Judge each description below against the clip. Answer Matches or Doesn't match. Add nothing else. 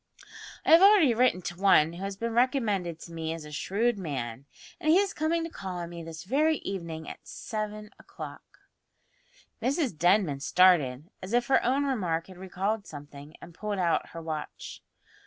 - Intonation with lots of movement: Matches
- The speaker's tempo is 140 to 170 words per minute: Doesn't match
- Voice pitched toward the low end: Doesn't match